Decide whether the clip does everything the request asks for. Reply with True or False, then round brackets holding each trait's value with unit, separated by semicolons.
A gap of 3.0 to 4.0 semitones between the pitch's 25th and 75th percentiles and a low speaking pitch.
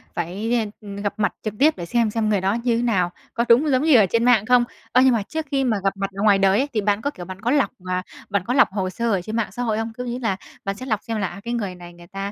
False (3.6 semitones; 215 Hz)